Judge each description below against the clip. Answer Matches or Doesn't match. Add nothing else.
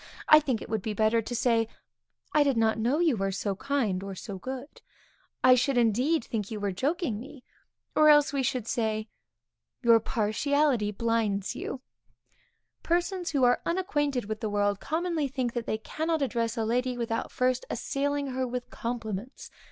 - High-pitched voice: Matches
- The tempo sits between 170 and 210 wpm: Matches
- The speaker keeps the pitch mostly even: Doesn't match